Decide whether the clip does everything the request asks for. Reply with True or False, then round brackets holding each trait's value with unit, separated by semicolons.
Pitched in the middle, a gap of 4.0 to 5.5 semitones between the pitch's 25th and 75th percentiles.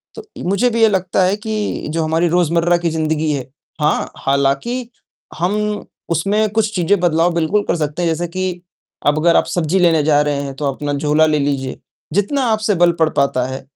True (170 Hz; 4.7 semitones)